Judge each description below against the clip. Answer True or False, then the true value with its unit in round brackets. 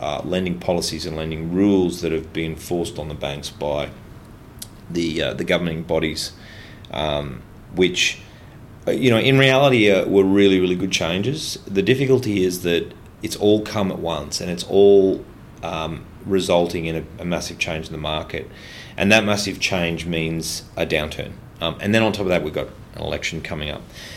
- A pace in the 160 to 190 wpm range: True (180 wpm)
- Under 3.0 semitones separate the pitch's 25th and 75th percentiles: False (4.2 semitones)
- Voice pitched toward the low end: True (90 Hz)